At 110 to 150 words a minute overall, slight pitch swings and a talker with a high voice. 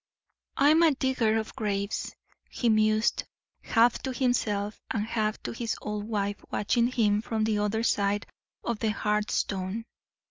Yes: average, 145 wpm; narrow, 2.1 semitones; high, 215 Hz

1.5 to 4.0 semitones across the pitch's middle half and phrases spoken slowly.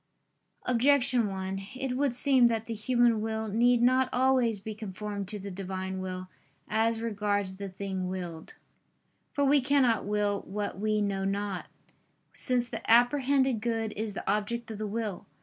No: average, 3.4 semitones; average, 160 wpm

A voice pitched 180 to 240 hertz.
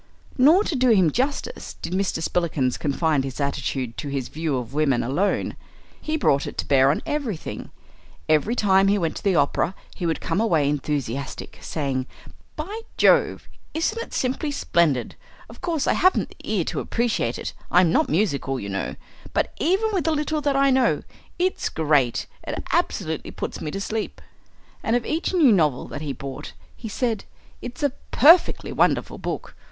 Yes: medium, 185 Hz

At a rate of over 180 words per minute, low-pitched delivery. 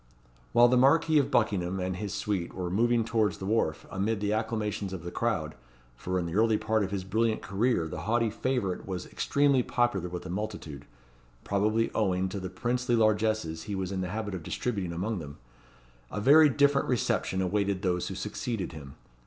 Yes: average, 190 wpm; low, 105 Hz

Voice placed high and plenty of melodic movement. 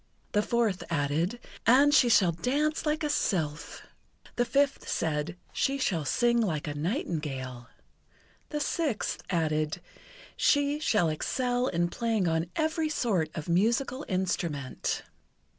Yes: high, 200 Hz; wide, 8.6 semitones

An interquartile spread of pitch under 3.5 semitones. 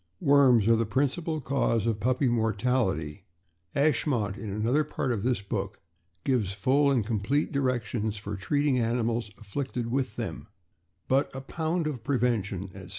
No: average, 4.4 semitones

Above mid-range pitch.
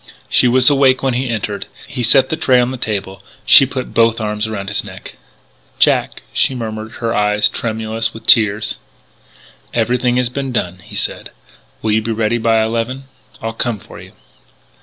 No: low, 115 Hz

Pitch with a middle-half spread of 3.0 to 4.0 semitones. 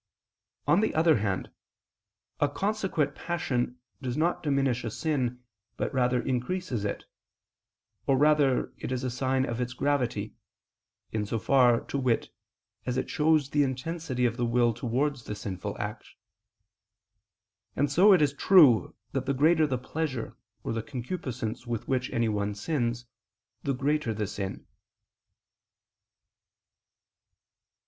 Yes: average, 3.7 semitones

